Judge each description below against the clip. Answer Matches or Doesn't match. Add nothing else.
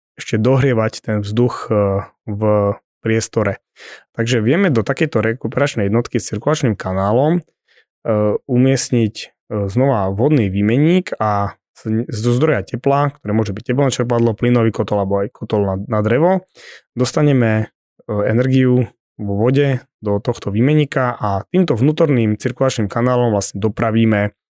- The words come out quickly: Doesn't match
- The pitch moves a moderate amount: Matches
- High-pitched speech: Doesn't match